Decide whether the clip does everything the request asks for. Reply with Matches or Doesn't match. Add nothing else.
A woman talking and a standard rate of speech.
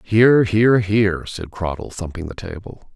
Doesn't match